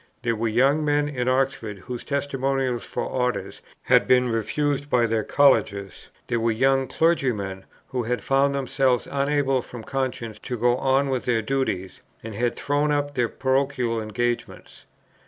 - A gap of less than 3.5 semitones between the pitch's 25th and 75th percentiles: Yes, average, 2.9 semitones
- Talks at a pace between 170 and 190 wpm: No, average, 155 wpm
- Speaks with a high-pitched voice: No, low, 125 Hz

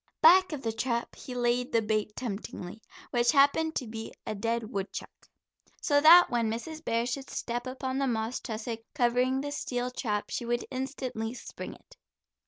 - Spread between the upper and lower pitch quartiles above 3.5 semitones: No, average, 3.0 semitones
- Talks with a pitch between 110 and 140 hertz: No, high, 245 Hz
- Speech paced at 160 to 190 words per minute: Yes, average, 175 wpm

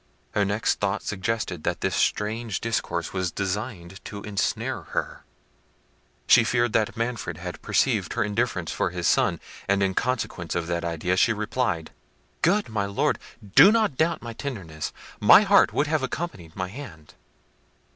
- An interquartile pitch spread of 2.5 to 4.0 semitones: No, average, 4.8 semitones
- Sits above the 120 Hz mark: No, low, 105 Hz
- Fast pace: No, average, 155 wpm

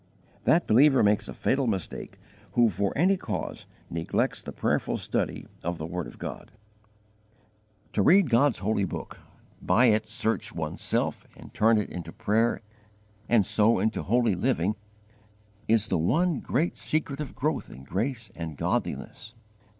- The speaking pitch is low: Yes, low, 110 Hz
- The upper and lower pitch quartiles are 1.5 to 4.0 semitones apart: No, average, 5.3 semitones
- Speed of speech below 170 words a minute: Yes, average, 150 wpm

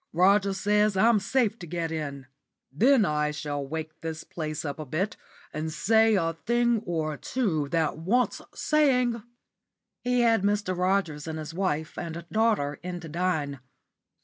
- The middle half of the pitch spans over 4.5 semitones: Yes, wide, 5.6 semitones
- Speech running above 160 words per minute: No, average, 155 wpm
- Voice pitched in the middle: Yes, medium, 175 Hz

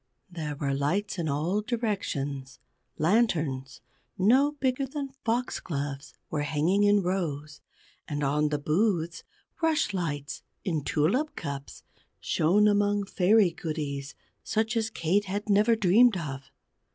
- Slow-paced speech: Yes, slow, 120 wpm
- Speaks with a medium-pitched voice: Yes, medium, 175 Hz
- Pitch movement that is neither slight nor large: No, wide, 6.3 semitones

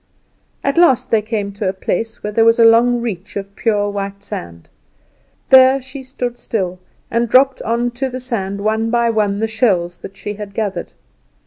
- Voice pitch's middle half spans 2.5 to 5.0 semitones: Yes, average, 3.3 semitones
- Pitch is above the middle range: Yes, high, 220 Hz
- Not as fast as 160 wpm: No, average, 185 wpm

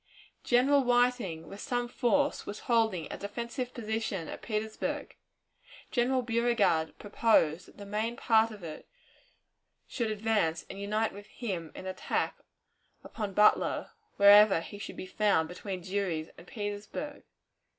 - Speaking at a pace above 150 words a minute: No, average, 140 wpm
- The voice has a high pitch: Yes, high, 210 Hz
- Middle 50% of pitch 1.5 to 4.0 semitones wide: Yes, average, 3.6 semitones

